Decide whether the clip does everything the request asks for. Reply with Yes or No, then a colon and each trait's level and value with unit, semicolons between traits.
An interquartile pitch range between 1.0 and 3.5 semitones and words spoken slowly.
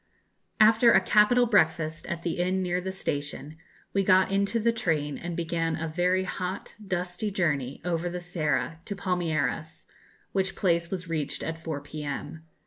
No: average, 2.9 semitones; average, 160 wpm